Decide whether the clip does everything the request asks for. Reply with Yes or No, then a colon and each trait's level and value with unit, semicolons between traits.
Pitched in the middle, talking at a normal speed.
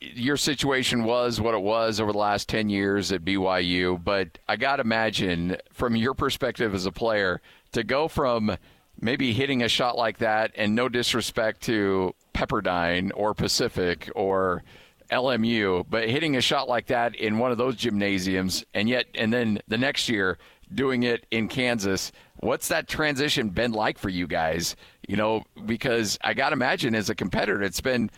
No: low, 110 Hz; average, 180 wpm